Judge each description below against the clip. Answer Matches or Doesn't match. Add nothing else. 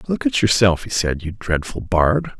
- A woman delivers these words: Doesn't match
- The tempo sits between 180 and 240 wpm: Matches